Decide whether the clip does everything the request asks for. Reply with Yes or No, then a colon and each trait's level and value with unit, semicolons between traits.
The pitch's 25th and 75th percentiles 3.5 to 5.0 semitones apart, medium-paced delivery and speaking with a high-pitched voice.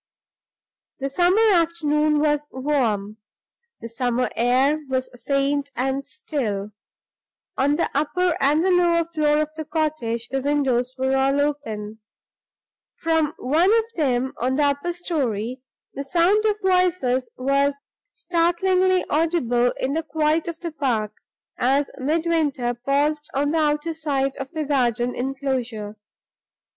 No: average, 3.8 semitones; slow, 130 wpm; very high, 285 Hz